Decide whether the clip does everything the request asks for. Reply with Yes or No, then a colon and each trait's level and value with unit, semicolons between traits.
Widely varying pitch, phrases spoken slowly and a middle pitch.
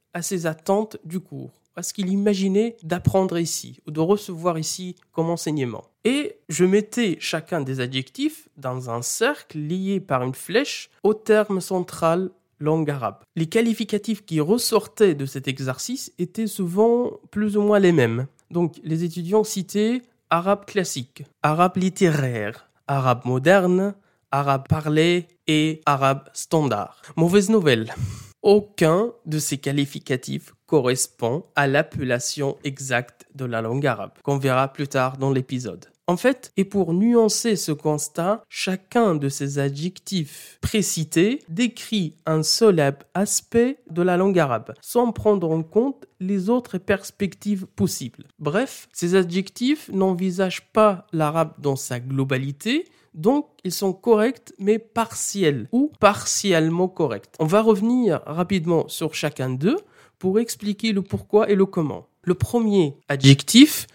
Yes: wide, 6.3 semitones; slow, 140 wpm; medium, 175 Hz